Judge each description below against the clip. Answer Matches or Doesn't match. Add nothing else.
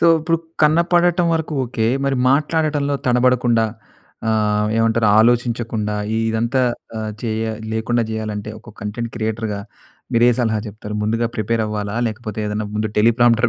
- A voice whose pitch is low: Matches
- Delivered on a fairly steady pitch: Matches